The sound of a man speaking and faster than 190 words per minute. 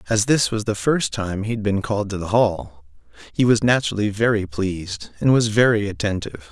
Yes: male; fast, 205 wpm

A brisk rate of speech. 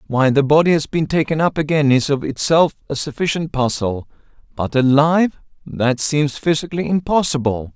No: average, 145 wpm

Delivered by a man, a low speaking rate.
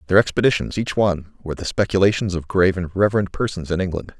No: male; average, 200 wpm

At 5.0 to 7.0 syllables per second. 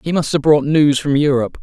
Yes: 6.0 syllables/s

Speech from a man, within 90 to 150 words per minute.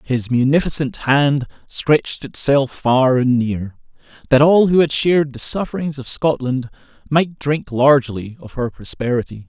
Yes: male; average, 145 wpm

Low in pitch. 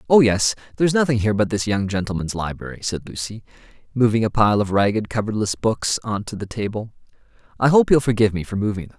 Yes: low, 110 Hz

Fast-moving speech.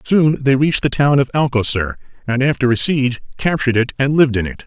Yes: fast, 220 wpm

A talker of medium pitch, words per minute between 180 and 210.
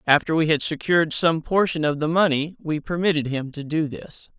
Yes: medium, 155 Hz; fast, 205 wpm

